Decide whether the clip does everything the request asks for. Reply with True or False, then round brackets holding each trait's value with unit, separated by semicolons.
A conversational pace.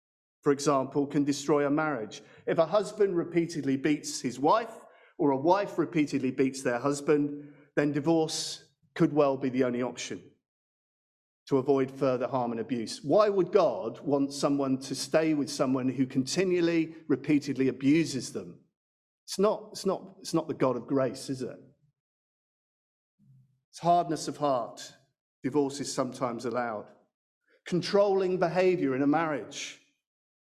True (145 wpm)